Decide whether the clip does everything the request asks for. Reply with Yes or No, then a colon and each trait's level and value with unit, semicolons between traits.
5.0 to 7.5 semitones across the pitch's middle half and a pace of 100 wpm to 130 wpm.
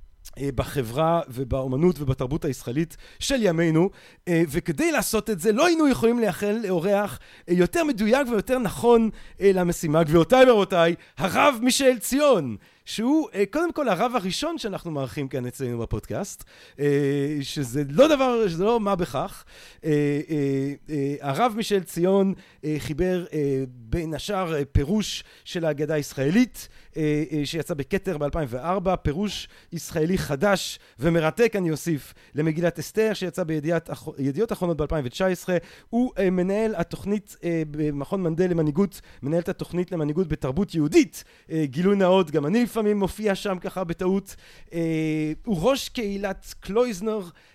Yes: average, 5.3 semitones; average, 115 wpm